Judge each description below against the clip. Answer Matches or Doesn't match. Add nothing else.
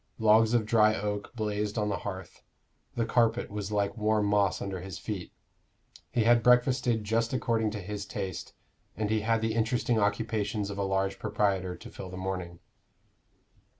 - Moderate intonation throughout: Doesn't match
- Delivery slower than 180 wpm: Matches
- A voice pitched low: Matches